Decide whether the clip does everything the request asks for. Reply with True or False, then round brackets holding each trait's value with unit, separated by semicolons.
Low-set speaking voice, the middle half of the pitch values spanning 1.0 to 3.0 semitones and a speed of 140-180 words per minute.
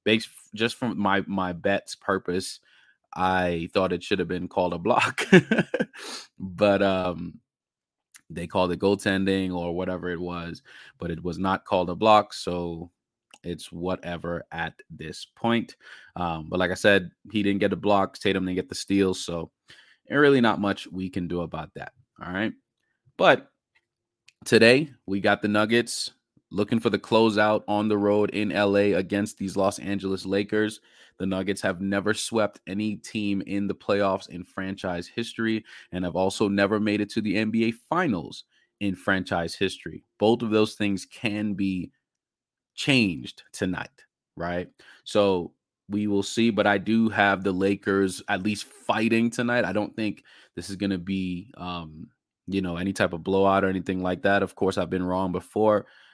True (100 Hz; 2.4 semitones; 170 wpm)